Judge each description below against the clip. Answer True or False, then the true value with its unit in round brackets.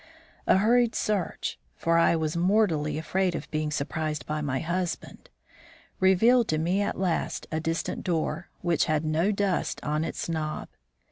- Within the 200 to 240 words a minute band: False (155 wpm)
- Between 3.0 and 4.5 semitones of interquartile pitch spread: True (3.5 semitones)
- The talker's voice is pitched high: False (165 Hz)